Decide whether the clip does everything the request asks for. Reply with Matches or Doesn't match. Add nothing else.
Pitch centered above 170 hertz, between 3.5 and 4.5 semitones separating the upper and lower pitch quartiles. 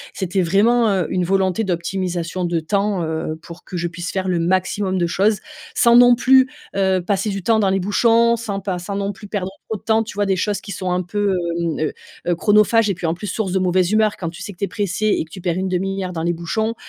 Doesn't match